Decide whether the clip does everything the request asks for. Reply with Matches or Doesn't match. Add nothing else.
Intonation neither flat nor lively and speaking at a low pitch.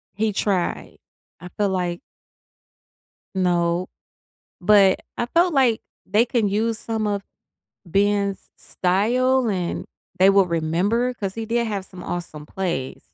Doesn't match